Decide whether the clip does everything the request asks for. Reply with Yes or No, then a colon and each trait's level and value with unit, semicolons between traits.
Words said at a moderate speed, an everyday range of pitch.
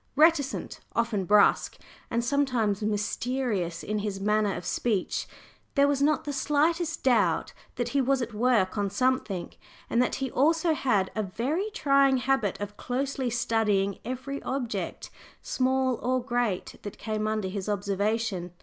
Yes: average, 150 wpm; average, 4.7 semitones